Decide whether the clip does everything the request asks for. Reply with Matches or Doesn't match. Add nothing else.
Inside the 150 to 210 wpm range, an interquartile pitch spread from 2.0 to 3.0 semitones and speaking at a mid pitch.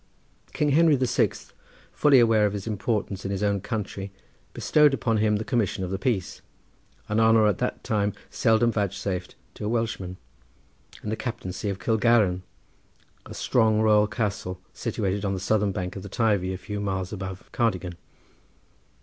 Doesn't match